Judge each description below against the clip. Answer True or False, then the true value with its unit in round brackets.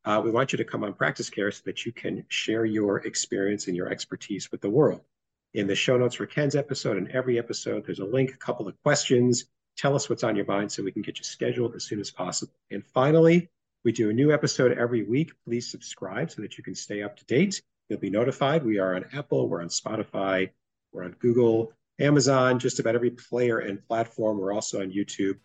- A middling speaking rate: False (230 wpm)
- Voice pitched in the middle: False (120 Hz)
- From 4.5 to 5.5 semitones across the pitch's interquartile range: True (4.8 semitones)